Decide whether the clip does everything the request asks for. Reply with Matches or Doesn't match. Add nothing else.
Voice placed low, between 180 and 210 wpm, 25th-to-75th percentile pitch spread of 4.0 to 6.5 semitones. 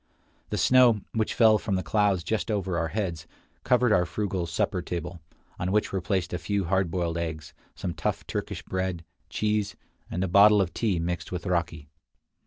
Doesn't match